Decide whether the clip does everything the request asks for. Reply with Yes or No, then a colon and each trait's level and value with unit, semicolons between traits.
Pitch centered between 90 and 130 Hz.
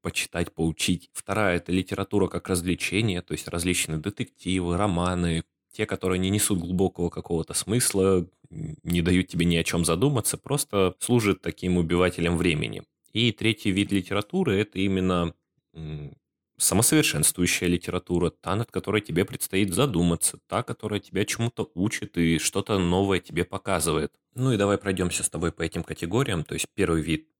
Yes: very low, 95 Hz